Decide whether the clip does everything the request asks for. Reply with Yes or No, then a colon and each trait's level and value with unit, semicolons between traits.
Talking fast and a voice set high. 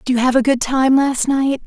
Yes: fast, 290 wpm; very high, 260 Hz